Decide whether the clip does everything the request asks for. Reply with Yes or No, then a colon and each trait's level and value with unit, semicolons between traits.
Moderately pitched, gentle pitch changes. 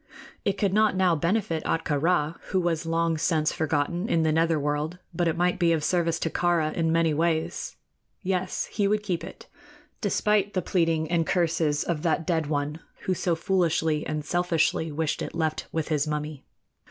Yes: medium, 165 Hz; narrow, 2.3 semitones